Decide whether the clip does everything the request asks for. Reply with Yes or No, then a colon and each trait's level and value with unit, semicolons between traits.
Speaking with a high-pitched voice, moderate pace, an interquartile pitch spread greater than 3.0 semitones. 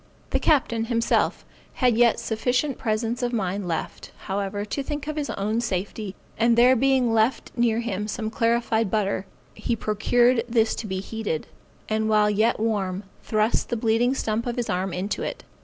No: high, 225 Hz; average, 170 wpm; narrow, 2.4 semitones